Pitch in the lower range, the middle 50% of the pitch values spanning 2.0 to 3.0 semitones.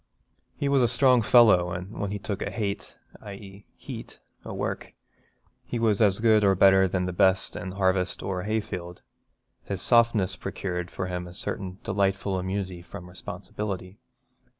Yes: very low, 95 Hz; narrow, 2.5 semitones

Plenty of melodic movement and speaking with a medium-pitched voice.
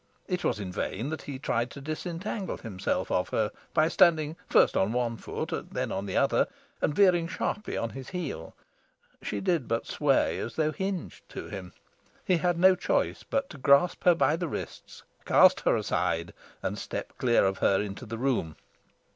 Yes: wide, 7.6 semitones; medium, 145 Hz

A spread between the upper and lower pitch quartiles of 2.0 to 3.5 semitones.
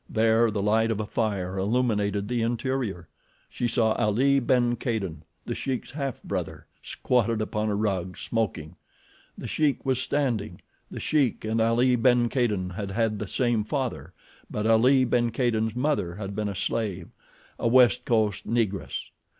Yes: average, 3.0 semitones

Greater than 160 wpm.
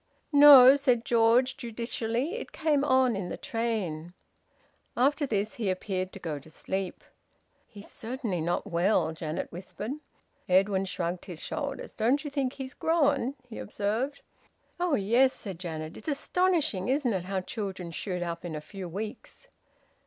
No: average, 155 wpm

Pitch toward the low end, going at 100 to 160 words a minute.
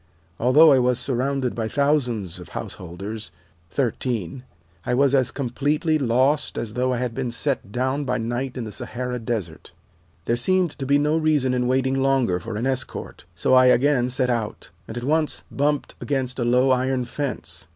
No: low, 125 Hz; average, 180 wpm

